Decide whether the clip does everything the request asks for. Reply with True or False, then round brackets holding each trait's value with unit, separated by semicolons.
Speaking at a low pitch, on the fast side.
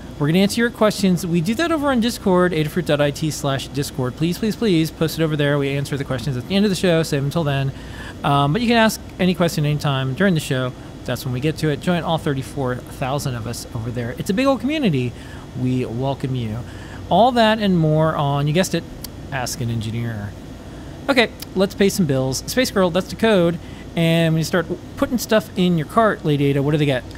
False (150 Hz; 230 wpm)